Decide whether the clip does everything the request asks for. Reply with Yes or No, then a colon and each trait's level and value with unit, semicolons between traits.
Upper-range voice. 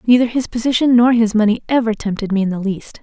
Yes: high, 225 Hz